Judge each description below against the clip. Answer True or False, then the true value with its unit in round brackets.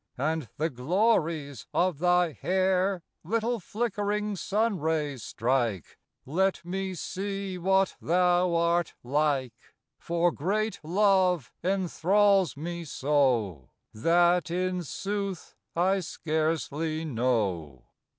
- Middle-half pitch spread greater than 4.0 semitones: True (4.6 semitones)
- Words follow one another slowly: True (100 wpm)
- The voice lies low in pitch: False (175 Hz)